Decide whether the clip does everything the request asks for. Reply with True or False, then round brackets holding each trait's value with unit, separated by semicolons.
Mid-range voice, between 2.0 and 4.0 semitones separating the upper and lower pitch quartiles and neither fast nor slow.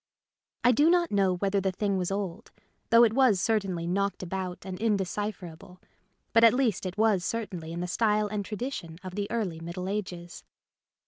False (195 Hz; 3.3 semitones; 185 wpm)